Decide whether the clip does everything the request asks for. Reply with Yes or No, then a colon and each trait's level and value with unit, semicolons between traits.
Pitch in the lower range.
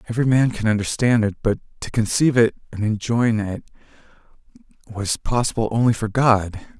Yes: low, 115 Hz